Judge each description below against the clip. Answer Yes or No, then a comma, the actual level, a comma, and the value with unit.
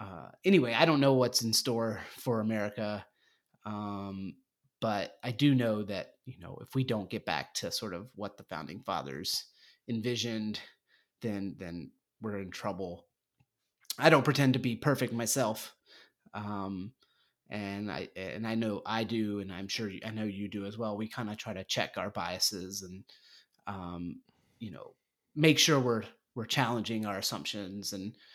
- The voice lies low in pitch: Yes, low, 110 Hz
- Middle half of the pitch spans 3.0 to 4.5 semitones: Yes, average, 3.4 semitones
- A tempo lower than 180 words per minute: Yes, average, 170 wpm